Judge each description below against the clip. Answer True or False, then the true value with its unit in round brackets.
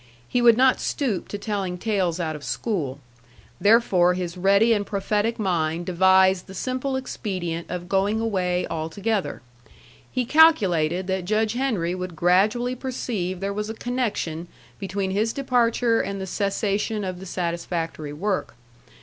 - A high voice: True (195 Hz)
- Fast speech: False (145 wpm)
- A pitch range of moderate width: True (4.0 semitones)